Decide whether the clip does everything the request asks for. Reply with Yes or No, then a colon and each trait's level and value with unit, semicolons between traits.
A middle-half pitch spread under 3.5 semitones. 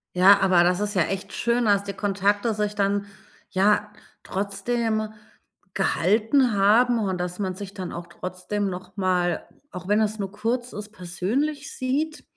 Yes: average, 2.7 semitones